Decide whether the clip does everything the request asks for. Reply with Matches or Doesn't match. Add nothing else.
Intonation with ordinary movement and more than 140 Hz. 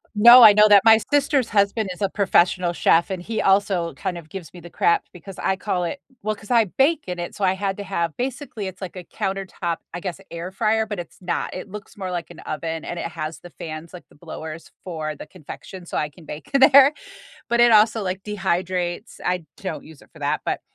Matches